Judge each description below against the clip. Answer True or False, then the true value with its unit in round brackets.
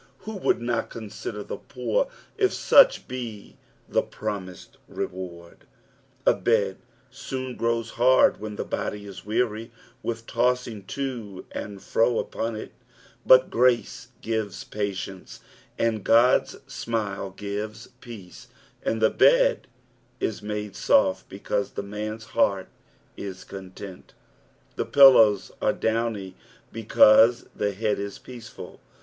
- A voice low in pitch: True (110 Hz)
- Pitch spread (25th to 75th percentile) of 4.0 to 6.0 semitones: False (2.9 semitones)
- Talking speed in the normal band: False (125 wpm)